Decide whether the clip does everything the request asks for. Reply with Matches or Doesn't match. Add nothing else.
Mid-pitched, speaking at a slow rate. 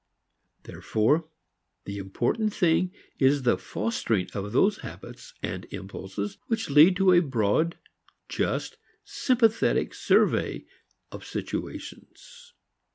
Matches